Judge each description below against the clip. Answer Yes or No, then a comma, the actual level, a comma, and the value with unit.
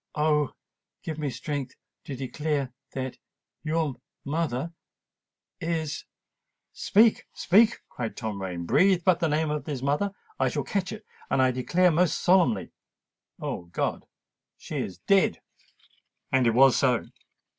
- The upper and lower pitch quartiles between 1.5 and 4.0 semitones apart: No, average, 4.9 semitones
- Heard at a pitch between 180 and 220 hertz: No, medium, 150 Hz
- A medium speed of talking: No, slow, 120 wpm